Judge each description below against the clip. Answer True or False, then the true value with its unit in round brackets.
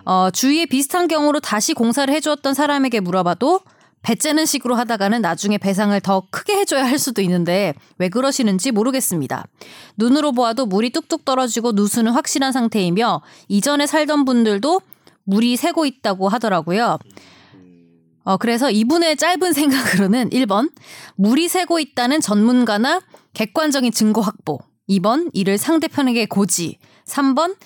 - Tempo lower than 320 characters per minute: False (340 characters per minute)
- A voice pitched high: True (240 Hz)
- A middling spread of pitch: False (6.6 semitones)